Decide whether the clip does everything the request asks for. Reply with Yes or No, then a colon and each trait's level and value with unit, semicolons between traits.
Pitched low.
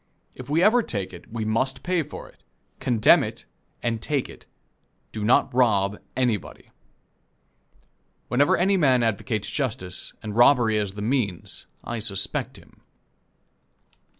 Yes: low, 120 Hz